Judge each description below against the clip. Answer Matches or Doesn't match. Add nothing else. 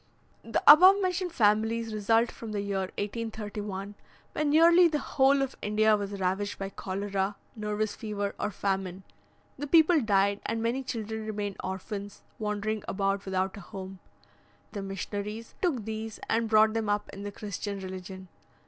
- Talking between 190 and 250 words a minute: Doesn't match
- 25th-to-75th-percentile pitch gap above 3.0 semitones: Doesn't match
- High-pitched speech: Matches